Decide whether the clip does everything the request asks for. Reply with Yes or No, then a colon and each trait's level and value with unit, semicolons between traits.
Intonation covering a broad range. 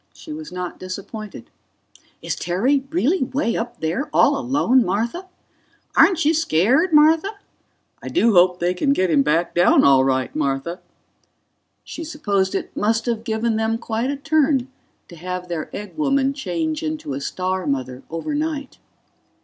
Yes: wide, 8.2 semitones